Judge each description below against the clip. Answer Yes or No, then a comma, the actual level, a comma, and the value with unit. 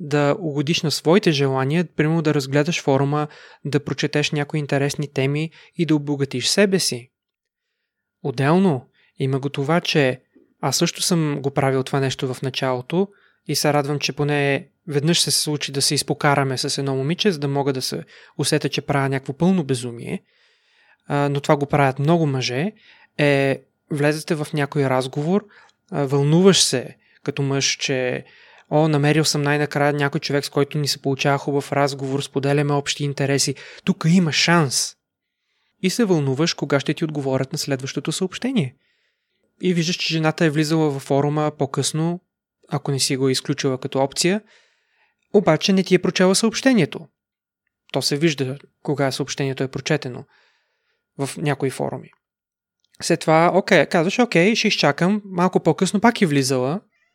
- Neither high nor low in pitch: Yes, medium, 145 Hz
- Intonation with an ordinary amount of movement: Yes, average, 3.5 semitones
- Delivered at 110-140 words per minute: No, average, 155 wpm